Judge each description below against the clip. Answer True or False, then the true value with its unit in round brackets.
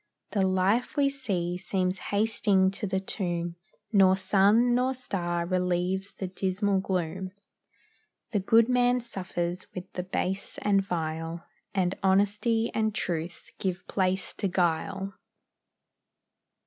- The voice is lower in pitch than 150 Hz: False (190 Hz)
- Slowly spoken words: True (120 wpm)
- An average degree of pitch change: False (2.3 semitones)